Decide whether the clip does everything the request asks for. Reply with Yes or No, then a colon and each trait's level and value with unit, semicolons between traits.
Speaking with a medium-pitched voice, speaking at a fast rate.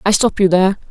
No: high, 195 Hz; fast, 265 wpm